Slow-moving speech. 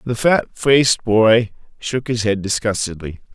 No: average, 145 wpm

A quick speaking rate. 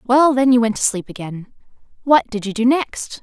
Yes: fast, 225 wpm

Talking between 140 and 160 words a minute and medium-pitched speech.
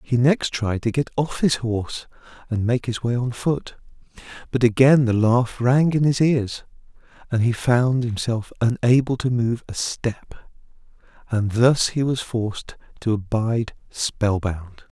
No: average, 155 wpm; low, 120 Hz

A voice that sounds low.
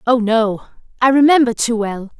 No: high, 235 Hz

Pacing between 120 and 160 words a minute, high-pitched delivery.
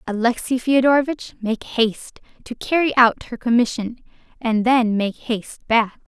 Yes: slow, 135 wpm; high, 235 Hz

